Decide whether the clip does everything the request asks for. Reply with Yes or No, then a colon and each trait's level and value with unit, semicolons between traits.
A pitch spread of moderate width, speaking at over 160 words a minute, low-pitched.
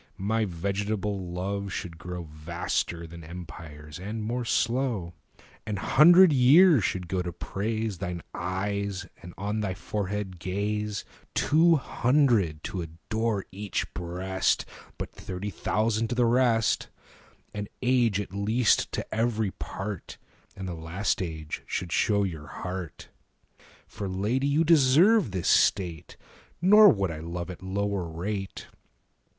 No: average, 4.0 semitones; slow, 135 wpm; low, 100 Hz